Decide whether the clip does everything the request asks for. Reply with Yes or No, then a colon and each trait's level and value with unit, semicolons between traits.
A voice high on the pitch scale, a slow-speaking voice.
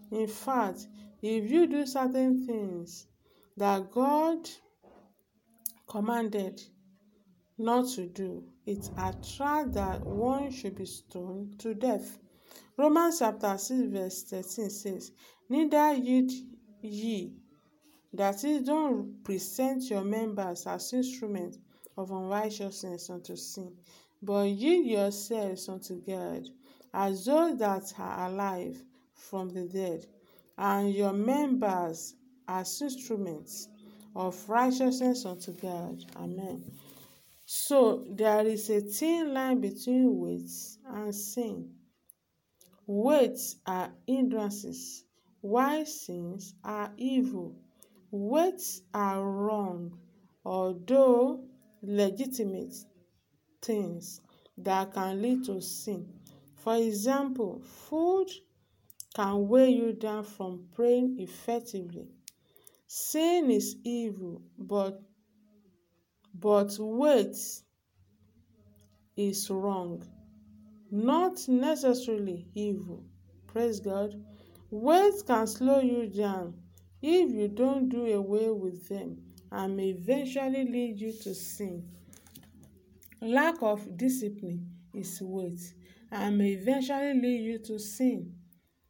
Yes: high, 210 Hz; slow, 95 wpm